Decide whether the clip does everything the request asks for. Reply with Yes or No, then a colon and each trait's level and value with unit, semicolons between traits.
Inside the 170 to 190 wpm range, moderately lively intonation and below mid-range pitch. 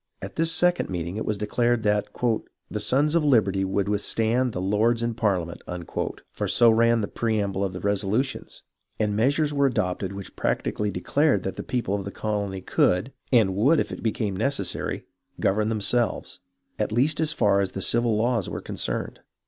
Yes: average, 180 wpm; average, 3.6 semitones; low, 110 Hz